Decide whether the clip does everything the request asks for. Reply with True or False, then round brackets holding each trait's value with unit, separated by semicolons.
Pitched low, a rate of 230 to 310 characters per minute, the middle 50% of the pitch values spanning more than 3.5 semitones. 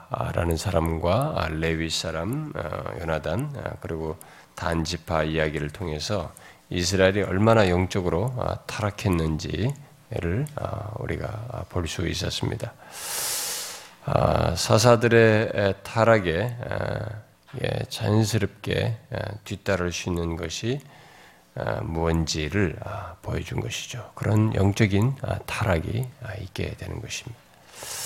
False (105 Hz; 210 characters per minute; 5.5 semitones)